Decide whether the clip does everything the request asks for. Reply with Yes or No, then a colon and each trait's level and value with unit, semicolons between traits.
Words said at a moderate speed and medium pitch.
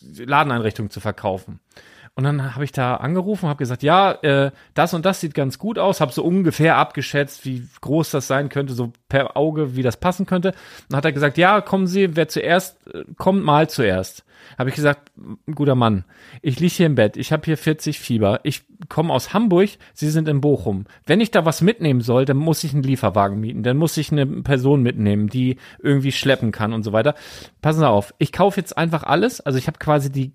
No: fast, 215 wpm; medium, 145 Hz